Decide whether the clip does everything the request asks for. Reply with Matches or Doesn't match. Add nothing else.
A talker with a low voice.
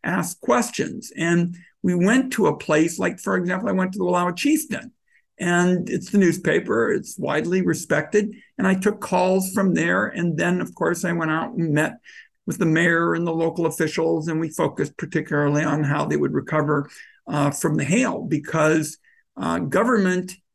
Doesn't match